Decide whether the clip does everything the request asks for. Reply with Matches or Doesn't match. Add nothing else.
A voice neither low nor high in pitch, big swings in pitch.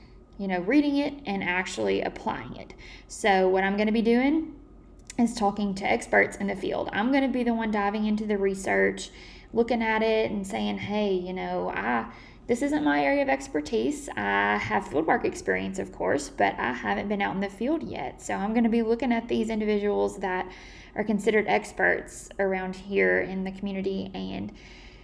Doesn't match